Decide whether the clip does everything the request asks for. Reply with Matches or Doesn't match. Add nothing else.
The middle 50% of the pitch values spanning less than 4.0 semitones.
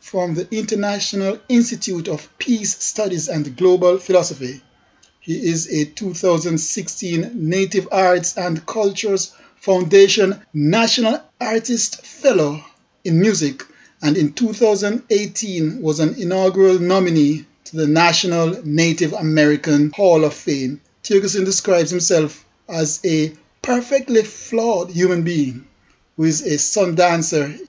Doesn't match